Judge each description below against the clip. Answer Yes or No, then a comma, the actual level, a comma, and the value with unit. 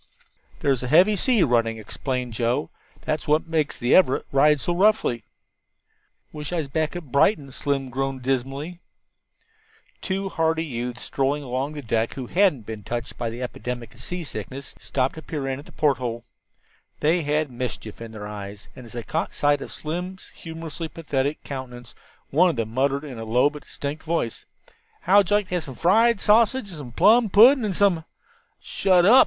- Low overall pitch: No, medium, 145 Hz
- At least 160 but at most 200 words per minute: Yes, average, 185 wpm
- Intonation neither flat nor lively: No, wide, 5.7 semitones